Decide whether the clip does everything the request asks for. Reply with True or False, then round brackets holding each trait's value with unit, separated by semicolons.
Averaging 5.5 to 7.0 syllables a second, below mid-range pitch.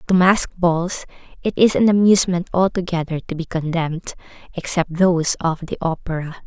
False (6.0 syllables/s; 175 Hz)